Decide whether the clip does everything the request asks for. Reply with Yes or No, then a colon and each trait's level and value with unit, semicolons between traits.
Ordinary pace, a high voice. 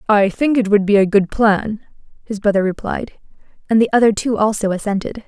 Yes: average, 195 wpm; high, 210 Hz